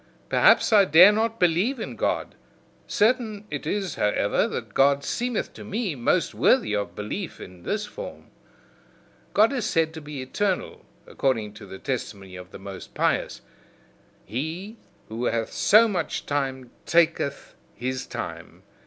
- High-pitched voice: No, medium, 160 Hz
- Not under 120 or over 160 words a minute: Yes, average, 145 wpm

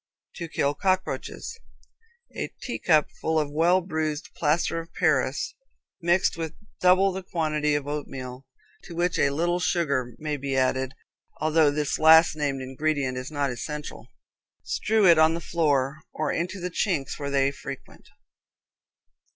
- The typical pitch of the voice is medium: Yes, medium, 155 Hz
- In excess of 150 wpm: No, average, 145 wpm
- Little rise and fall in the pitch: No, average, 3.4 semitones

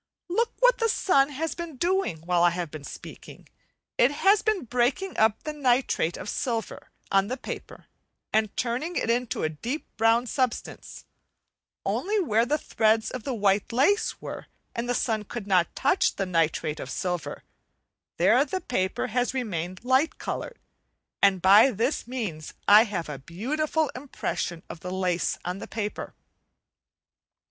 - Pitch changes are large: Yes, wide, 7.0 semitones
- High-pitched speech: Yes, high, 230 Hz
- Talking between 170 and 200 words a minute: No, average, 155 wpm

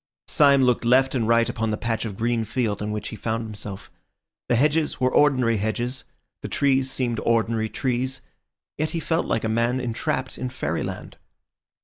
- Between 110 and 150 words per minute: No, average, 175 wpm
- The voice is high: No, low, 120 Hz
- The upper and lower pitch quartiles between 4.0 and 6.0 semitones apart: No, average, 2.8 semitones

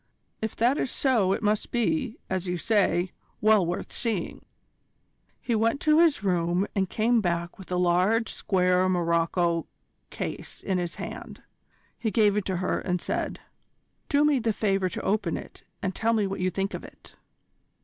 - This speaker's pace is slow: No, average, 175 wpm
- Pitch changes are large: No, average, 3.9 semitones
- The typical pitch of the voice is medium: No, high, 195 Hz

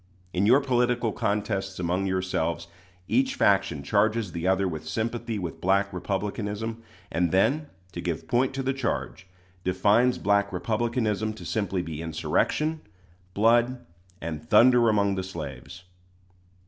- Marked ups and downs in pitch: No, average, 4.3 semitones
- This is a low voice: Yes, low, 100 Hz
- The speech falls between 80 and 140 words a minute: Yes, slow, 135 wpm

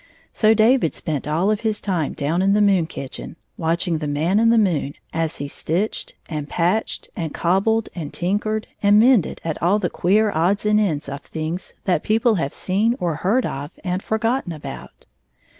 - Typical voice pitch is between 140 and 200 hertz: Yes, medium, 185 Hz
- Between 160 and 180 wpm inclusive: No, average, 190 wpm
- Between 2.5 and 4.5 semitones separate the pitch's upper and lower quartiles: No, average, 5.0 semitones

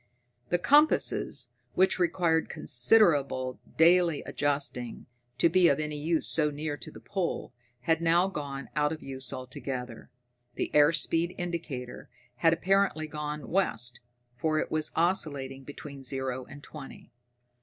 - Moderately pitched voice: Yes, medium, 150 Hz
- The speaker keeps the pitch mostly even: No, average, 3.9 semitones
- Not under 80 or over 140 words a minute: Yes, slow, 135 wpm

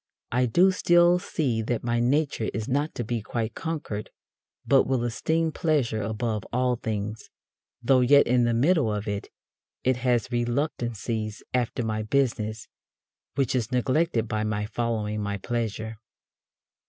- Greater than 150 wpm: No, average, 145 wpm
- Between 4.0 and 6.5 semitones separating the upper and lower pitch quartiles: No, average, 3.5 semitones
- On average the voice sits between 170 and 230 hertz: No, low, 120 Hz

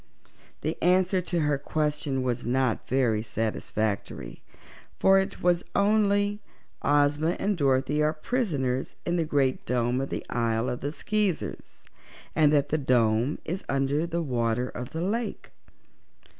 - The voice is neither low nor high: Yes, medium, 145 Hz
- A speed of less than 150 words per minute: Yes, average, 140 wpm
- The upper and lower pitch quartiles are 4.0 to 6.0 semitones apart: Yes, wide, 5.6 semitones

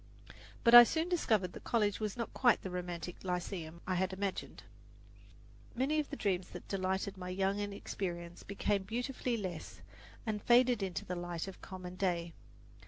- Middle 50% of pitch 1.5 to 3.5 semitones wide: No, average, 4.1 semitones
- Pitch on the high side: Yes, high, 195 Hz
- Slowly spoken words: No, average, 170 wpm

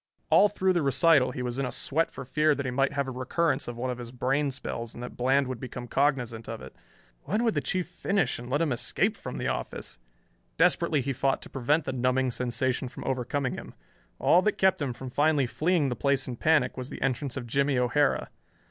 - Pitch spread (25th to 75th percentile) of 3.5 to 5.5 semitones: No, average, 2.8 semitones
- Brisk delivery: Yes, fast, 230 wpm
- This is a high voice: No, low, 135 Hz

